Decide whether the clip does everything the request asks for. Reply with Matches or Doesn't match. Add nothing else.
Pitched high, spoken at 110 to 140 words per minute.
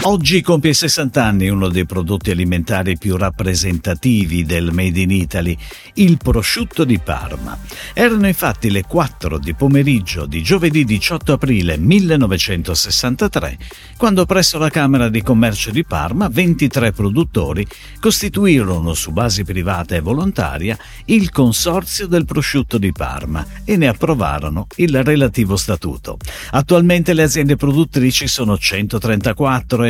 Doesn't match